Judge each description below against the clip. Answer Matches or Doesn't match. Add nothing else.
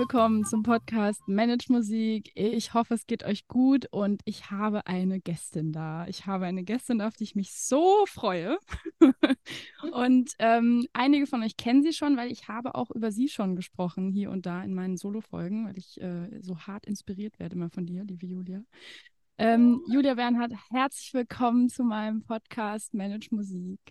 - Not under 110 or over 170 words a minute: Doesn't match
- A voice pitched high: Matches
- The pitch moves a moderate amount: Matches